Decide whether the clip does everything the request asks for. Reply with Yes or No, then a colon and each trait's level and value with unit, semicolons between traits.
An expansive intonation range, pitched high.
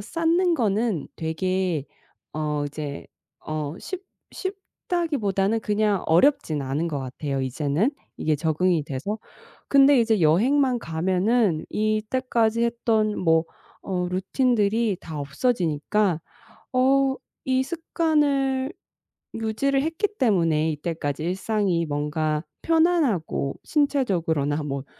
Yes: wide, 8.6 semitones; high, 200 Hz